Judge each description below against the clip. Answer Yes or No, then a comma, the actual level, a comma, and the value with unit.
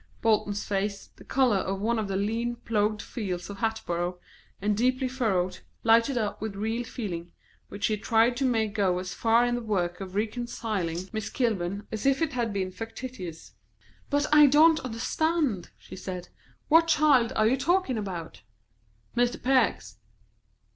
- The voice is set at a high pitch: Yes, high, 220 Hz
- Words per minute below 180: Yes, average, 160 wpm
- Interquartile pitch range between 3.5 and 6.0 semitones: Yes, average, 4.1 semitones